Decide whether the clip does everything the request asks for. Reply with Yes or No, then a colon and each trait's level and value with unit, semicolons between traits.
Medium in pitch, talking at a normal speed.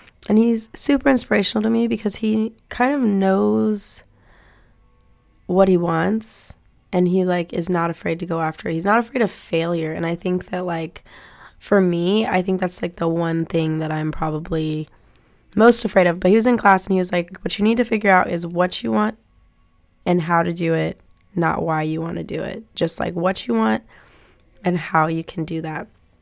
No: medium, 175 Hz; fast, 210 wpm